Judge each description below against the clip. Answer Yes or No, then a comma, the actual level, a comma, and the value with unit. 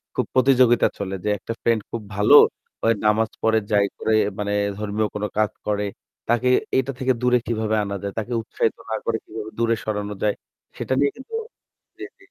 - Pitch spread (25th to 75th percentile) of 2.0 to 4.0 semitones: Yes, narrow, 2.4 semitones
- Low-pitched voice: Yes, low, 110 Hz